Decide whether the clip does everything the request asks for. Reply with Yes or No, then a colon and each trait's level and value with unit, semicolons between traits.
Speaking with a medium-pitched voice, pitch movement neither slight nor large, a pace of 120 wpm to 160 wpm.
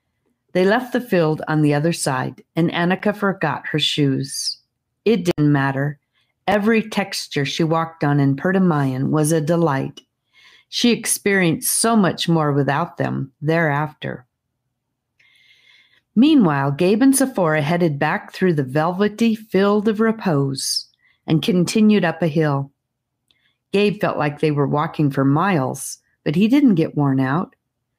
No: medium, 160 Hz; wide, 5.9 semitones; average, 140 wpm